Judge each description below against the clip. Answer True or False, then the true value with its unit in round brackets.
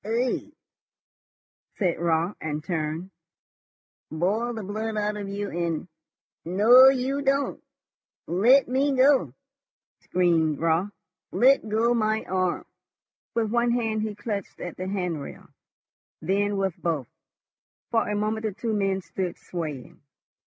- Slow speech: True (130 wpm)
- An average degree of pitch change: True (4.6 semitones)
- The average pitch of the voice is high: True (205 Hz)